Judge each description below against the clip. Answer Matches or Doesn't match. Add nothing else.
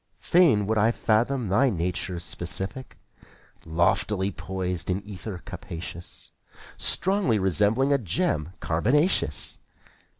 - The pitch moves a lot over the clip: Matches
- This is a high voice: Doesn't match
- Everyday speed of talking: Doesn't match